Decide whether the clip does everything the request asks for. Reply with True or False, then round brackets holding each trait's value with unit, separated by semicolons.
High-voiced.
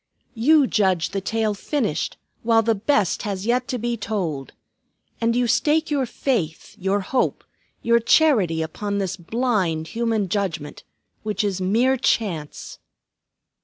True (215 Hz)